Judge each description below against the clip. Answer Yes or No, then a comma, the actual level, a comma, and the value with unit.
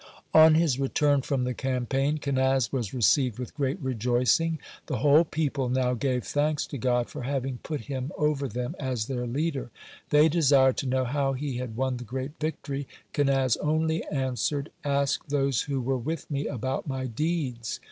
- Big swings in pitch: No, narrow, 2.6 semitones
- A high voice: No, low, 135 Hz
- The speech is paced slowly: No, average, 175 wpm